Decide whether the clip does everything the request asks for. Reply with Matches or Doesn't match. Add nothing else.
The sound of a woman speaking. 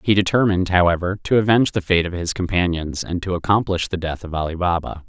Doesn't match